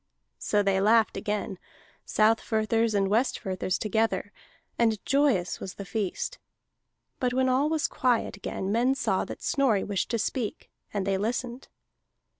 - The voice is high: Yes, high, 220 Hz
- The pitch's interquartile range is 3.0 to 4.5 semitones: Yes, average, 3.7 semitones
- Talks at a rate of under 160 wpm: Yes, average, 140 wpm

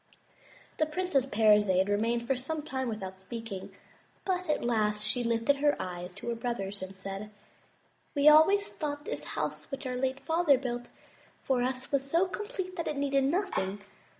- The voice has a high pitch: Yes, very high, 255 Hz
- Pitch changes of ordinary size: No, wide, 6.0 semitones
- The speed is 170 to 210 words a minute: Yes, average, 180 wpm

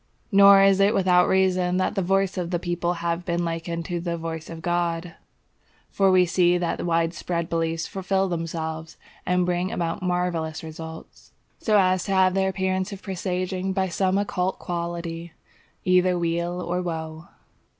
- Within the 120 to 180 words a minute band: Yes, average, 165 wpm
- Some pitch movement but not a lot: No, narrow, 1.9 semitones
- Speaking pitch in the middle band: Yes, medium, 175 Hz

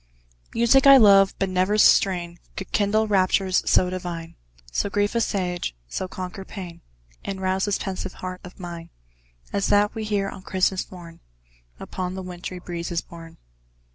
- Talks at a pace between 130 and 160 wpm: Yes, average, 155 wpm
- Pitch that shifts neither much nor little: No, narrow, 2.1 semitones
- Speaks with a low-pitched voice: No, medium, 185 Hz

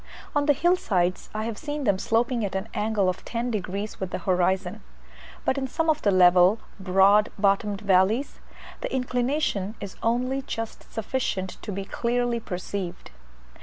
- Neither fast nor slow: Yes, average, 165 wpm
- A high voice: Yes, high, 210 Hz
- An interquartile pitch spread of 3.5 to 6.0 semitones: Yes, average, 4.5 semitones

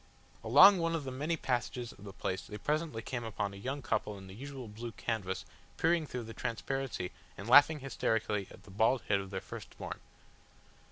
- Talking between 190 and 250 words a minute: Yes, average, 200 wpm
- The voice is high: No, low, 120 Hz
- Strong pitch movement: No, average, 5.0 semitones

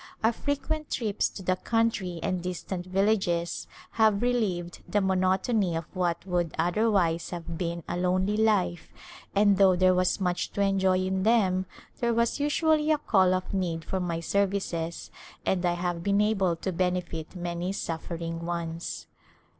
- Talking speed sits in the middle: Yes, average, 160 wpm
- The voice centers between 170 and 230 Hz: Yes, medium, 185 Hz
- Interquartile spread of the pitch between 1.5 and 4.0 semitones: Yes, average, 2.8 semitones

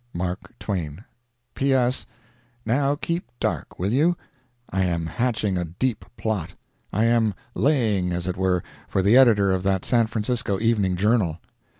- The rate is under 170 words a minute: Yes, average, 140 wpm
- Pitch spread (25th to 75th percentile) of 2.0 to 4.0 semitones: No, average, 4.8 semitones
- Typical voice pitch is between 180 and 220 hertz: No, low, 105 Hz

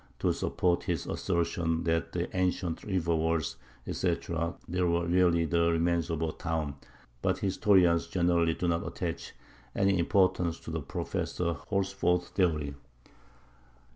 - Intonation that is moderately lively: No, narrow, 1.6 semitones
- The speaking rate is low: Yes, slow, 130 wpm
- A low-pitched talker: Yes, very low, 85 Hz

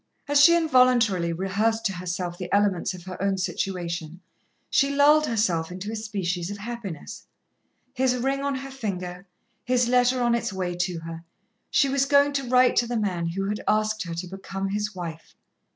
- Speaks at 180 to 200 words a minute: Yes, average, 185 wpm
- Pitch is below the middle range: No, high, 205 Hz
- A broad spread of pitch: Yes, wide, 5.7 semitones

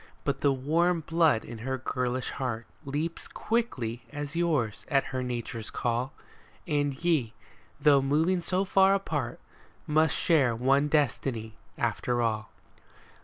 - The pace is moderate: No, slow, 130 wpm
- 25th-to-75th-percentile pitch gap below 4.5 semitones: No, average, 4.8 semitones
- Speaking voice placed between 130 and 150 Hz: Yes, medium, 140 Hz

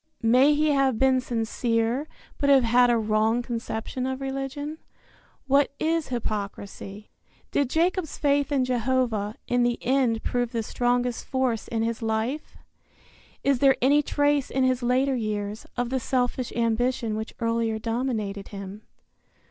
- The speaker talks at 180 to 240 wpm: No, average, 145 wpm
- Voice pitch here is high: Yes, high, 245 Hz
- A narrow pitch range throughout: No, average, 3.1 semitones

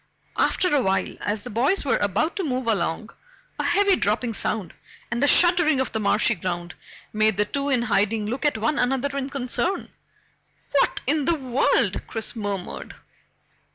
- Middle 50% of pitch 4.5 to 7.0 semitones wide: Yes, average, 5.2 semitones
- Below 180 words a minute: Yes, average, 170 wpm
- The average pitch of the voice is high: Yes, high, 245 Hz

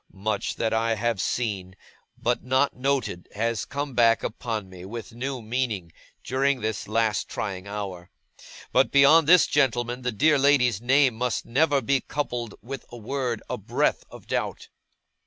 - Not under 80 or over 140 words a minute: No, average, 155 wpm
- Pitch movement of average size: Yes, average, 3.9 semitones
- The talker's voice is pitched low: Yes, low, 120 Hz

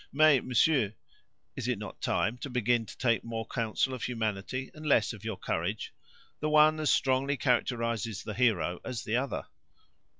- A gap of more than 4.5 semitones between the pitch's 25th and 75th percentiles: No, average, 3.3 semitones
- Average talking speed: Yes, average, 170 wpm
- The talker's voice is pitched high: No, low, 120 Hz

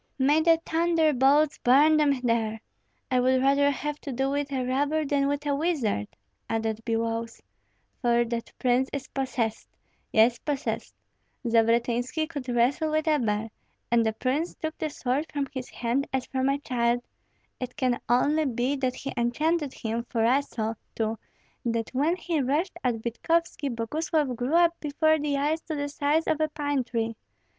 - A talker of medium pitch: No, very high, 270 Hz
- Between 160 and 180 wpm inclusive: Yes, average, 170 wpm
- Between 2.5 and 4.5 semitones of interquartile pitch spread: Yes, average, 4.0 semitones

